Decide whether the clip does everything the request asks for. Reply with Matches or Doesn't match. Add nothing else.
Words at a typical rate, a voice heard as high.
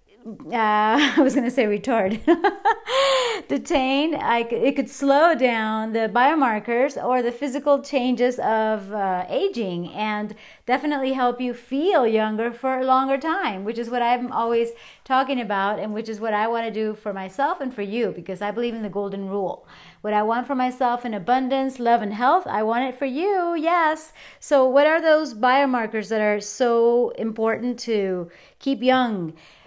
Matches